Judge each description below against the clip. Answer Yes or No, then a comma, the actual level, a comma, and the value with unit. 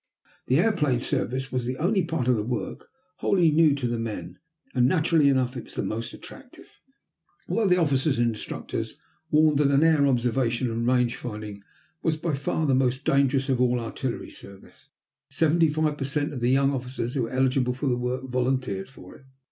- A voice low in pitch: Yes, low, 130 Hz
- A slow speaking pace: No, average, 190 wpm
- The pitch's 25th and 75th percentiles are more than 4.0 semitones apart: No, average, 3.3 semitones